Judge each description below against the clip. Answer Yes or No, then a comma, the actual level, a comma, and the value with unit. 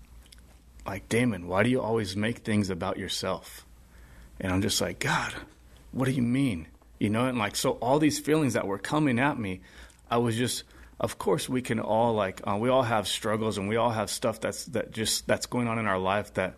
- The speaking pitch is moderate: No, low, 105 Hz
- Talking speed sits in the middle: No, fast, 220 wpm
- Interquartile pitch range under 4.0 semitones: No, average, 5.3 semitones